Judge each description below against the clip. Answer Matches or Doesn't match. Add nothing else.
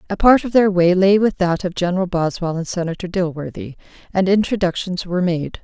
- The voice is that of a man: Doesn't match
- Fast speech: Doesn't match